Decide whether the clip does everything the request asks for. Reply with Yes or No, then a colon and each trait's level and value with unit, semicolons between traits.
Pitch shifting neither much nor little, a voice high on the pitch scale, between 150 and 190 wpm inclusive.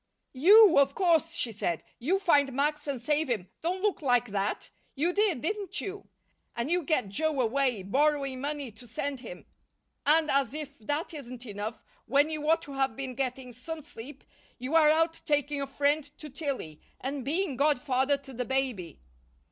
Yes: average, 3.7 semitones; very high, 280 Hz; average, 180 wpm